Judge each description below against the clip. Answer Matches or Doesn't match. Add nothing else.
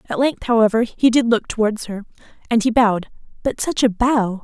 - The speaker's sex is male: Doesn't match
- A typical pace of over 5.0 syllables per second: Matches